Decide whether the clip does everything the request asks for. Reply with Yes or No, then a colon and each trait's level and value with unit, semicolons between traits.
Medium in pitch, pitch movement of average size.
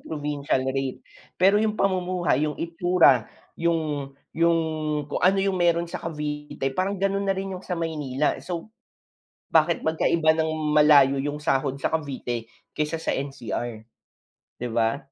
Yes: medium, 155 Hz; average, 4.0 semitones